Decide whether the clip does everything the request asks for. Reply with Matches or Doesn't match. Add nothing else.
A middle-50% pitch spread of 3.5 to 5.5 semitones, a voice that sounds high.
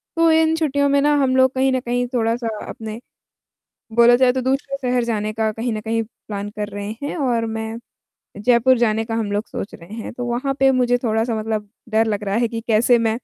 Doesn't match